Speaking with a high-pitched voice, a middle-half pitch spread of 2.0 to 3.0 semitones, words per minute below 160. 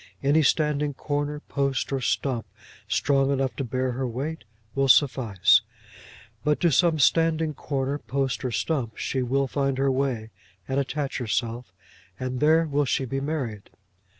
No: low, 135 Hz; narrow, 2.4 semitones; average, 150 wpm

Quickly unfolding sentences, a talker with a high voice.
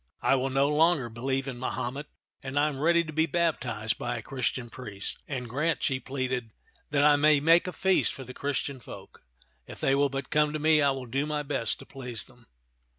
No: fast, 225 wpm; low, 135 Hz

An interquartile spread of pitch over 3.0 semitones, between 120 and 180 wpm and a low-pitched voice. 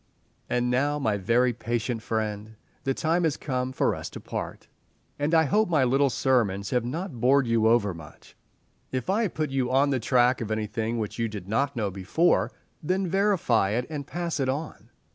No: average, 4.6 semitones; average, 195 wpm; low, 125 Hz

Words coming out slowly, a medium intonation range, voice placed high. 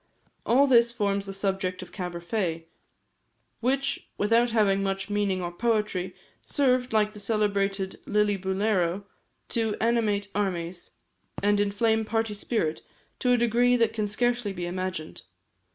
Yes: slow, 130 wpm; average, 3.0 semitones; high, 205 Hz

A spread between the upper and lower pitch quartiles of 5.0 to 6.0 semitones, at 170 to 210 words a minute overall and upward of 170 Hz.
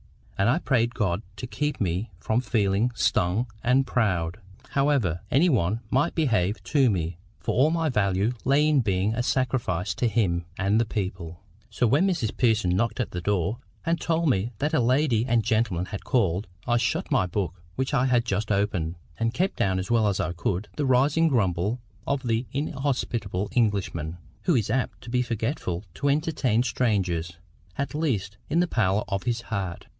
No: wide, 5.4 semitones; average, 185 wpm; low, 115 Hz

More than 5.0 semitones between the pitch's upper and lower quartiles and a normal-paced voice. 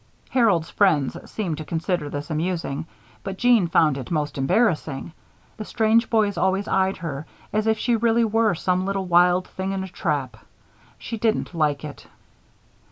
Yes: wide, 5.5 semitones; average, 165 wpm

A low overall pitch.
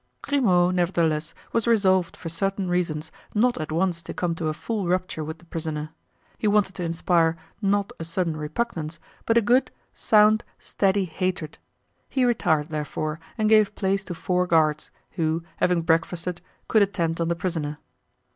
No: medium, 175 Hz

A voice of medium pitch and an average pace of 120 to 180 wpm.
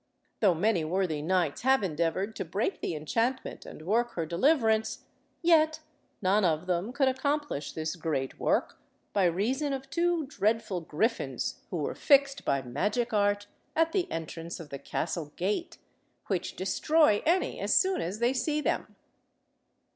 No: high, 205 Hz; average, 155 wpm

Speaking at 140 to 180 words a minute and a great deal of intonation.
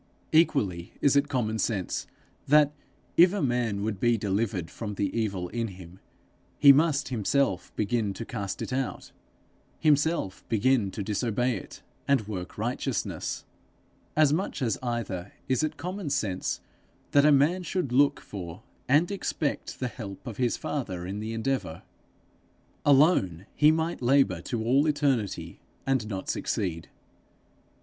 Yes: average, 145 wpm; wide, 6.1 semitones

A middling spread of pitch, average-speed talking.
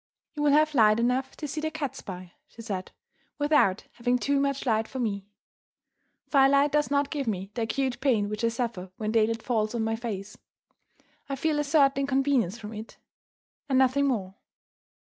Yes: average, 4.4 semitones; average, 180 wpm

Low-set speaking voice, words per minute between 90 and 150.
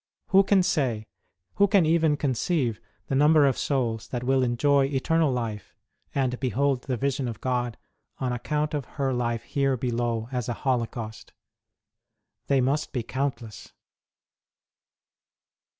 Yes: low, 130 Hz; average, 140 wpm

